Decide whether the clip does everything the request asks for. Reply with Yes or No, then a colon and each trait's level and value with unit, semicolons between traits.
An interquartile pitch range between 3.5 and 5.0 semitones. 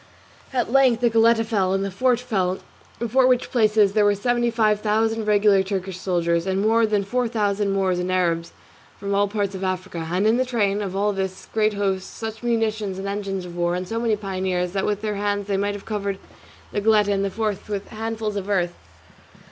No: narrow, 2.5 semitones